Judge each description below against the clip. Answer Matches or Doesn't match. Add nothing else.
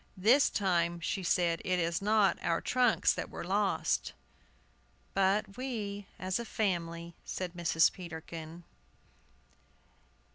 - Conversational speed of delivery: Doesn't match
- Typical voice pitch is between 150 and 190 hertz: Matches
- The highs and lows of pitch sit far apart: Doesn't match